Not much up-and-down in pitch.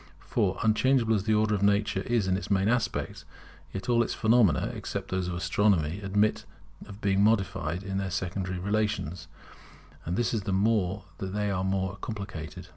Yes: narrow, 2.3 semitones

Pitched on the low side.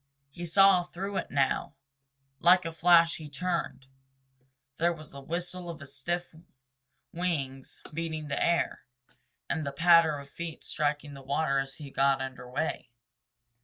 No: medium, 160 Hz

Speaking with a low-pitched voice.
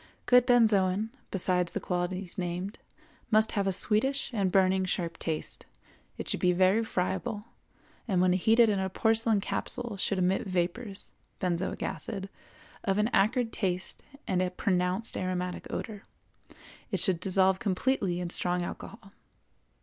No: high, 190 Hz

